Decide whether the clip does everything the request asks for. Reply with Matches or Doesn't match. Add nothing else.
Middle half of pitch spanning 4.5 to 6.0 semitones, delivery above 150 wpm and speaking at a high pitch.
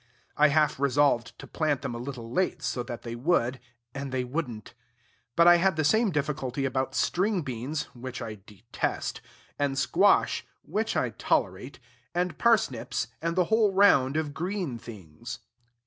Doesn't match